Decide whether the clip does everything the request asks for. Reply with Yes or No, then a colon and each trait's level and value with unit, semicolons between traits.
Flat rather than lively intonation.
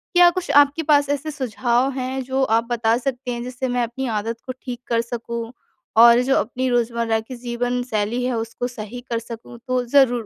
Yes: narrow, 1.9 semitones